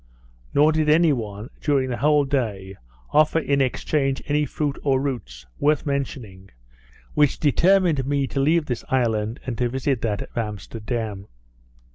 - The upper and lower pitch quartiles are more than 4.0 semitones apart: Yes, average, 4.4 semitones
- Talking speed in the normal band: Yes, average, 150 wpm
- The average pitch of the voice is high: No, low, 135 Hz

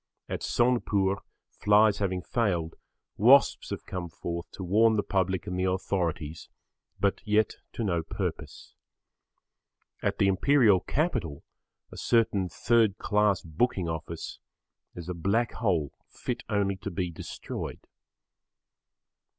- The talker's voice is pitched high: No, very low, 95 Hz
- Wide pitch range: No, average, 3.8 semitones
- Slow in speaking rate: Yes, slow, 125 wpm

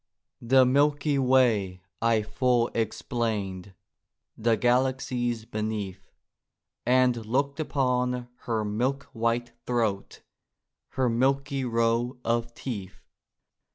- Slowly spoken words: Yes, slow, 90 wpm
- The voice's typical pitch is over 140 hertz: No, low, 120 Hz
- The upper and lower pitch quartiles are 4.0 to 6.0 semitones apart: No, narrow, 2.5 semitones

